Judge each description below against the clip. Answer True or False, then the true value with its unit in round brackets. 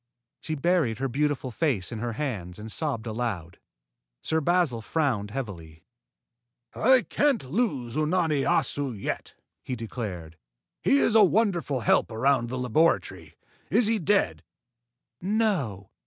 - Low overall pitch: True (130 Hz)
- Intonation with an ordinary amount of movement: False (7.5 semitones)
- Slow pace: True (130 wpm)